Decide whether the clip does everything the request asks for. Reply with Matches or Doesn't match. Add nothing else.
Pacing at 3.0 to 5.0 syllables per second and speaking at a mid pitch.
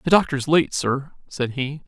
Matches